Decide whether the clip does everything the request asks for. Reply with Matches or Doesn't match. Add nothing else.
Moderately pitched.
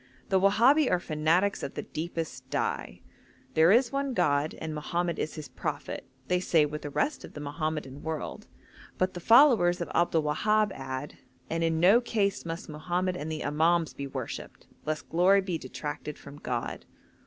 Matches